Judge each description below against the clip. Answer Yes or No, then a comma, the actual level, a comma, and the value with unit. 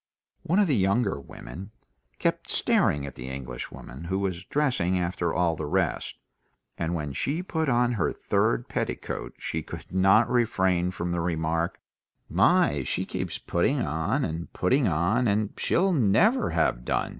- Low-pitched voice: Yes, very low, 95 Hz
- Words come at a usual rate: Yes, average, 155 wpm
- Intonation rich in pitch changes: Yes, wide, 6.6 semitones